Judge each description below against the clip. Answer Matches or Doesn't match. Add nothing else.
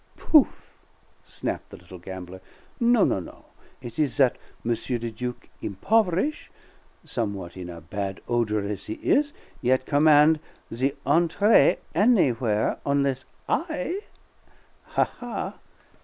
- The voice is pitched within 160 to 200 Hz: Doesn't match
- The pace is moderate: Doesn't match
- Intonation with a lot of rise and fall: Matches